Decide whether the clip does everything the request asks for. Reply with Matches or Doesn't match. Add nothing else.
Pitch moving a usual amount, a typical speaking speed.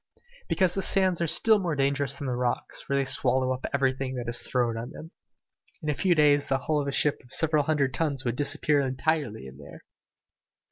Doesn't match